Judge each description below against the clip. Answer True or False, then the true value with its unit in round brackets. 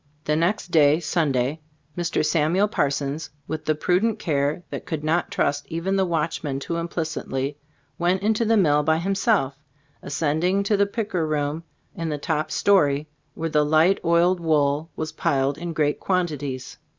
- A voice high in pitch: False (160 Hz)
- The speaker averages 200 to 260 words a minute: False (160 wpm)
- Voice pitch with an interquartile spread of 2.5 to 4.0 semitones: True (3.4 semitones)